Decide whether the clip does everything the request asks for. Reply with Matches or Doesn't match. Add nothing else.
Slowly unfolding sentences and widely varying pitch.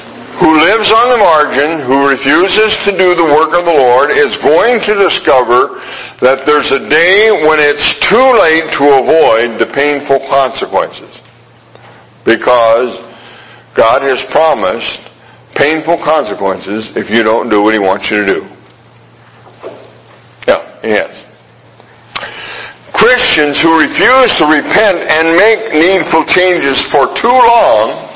Matches